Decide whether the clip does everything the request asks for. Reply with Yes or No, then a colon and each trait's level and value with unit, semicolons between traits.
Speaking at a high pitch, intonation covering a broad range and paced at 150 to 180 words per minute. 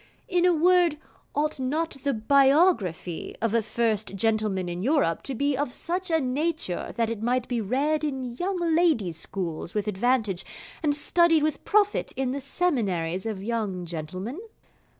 Yes: very high, 250 Hz; wide, 7.2 semitones; average, 160 wpm